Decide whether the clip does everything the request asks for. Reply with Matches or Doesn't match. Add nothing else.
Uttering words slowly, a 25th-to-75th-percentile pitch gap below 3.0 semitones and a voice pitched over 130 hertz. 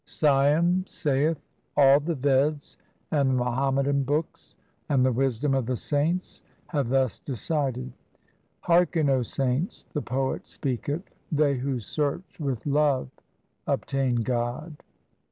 Matches